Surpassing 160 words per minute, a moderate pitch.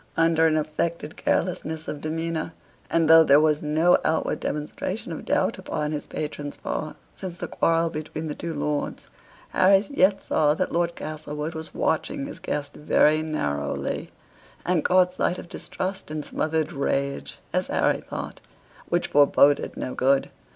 No: average, 155 wpm; medium, 155 Hz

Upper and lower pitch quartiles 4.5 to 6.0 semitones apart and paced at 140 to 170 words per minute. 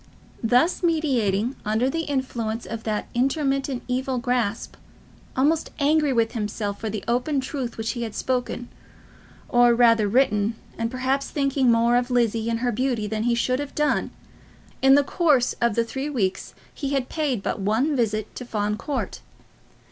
No: average, 3.2 semitones; average, 165 wpm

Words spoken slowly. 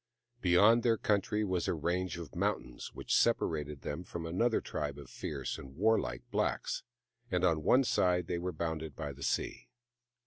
No: average, 170 wpm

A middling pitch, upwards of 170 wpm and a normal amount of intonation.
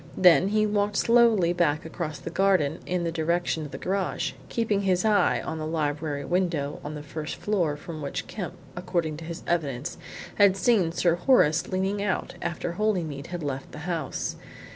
Yes: medium, 170 Hz; average, 180 wpm; average, 3.9 semitones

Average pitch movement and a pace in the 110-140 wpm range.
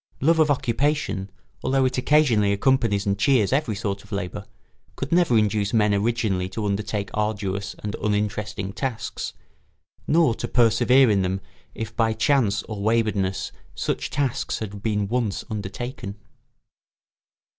Yes: average, 3.8 semitones; slow, 135 wpm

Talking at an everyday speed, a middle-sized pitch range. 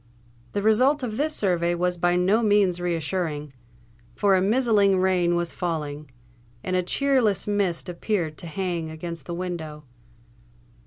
Yes: average, 145 wpm; average, 3.2 semitones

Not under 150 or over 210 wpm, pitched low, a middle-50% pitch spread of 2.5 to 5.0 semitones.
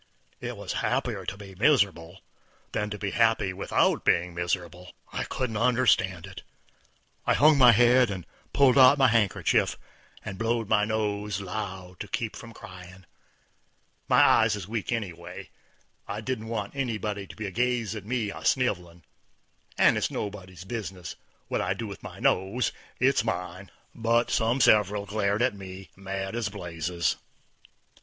Yes: average, 160 wpm; low, 105 Hz; average, 3.7 semitones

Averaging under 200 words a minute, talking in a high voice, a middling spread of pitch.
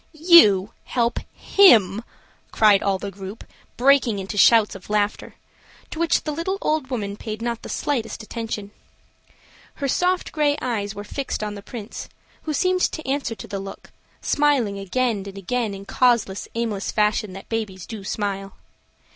Yes: average, 165 wpm; high, 220 Hz; average, 5.0 semitones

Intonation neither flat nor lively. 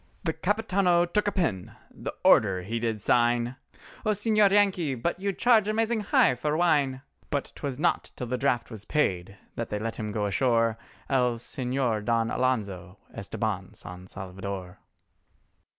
No: wide, 8.5 semitones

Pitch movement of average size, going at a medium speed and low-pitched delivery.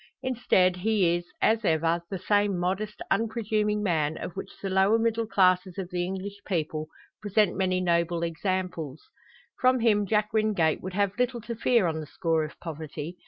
No: average, 3.8 semitones; average, 170 wpm; high, 190 Hz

